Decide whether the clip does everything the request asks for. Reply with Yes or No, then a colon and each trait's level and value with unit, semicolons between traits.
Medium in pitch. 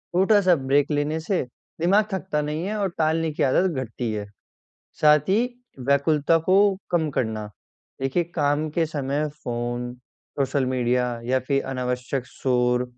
Yes: medium, 145 Hz